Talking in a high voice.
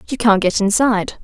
Yes: high, 215 Hz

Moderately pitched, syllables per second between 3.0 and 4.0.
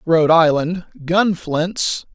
Yes: medium, 165 Hz; 3.3 syllables/s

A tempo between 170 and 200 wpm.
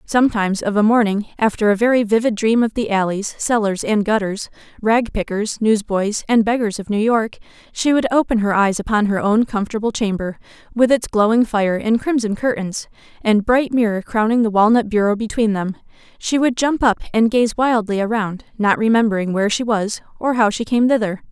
Yes: average, 185 wpm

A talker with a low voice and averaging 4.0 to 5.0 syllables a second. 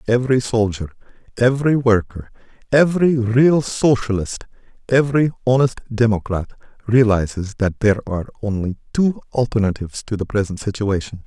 No: low, 115 Hz; 5.5 syllables/s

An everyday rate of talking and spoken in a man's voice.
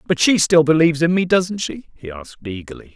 No: fast, 225 wpm; male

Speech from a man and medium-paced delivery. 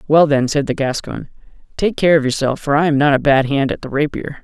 No: male; fast, 255 wpm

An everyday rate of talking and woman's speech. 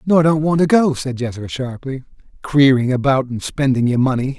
No: average, 190 wpm; male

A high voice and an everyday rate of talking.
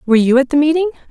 No: very high, 285 Hz; fast, 270 wpm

